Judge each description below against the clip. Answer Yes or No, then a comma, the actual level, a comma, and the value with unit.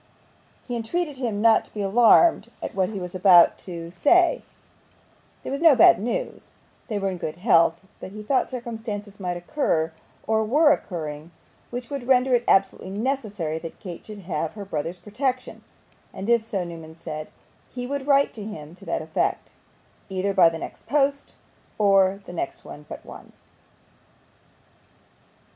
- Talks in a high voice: Yes, high, 205 Hz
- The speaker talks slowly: No, average, 160 wpm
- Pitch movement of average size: No, wide, 5.9 semitones